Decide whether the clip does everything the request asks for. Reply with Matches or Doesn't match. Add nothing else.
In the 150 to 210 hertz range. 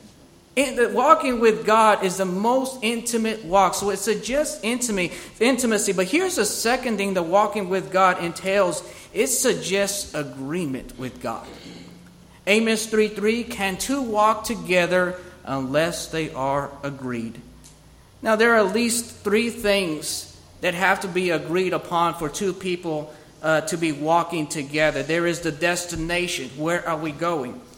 Matches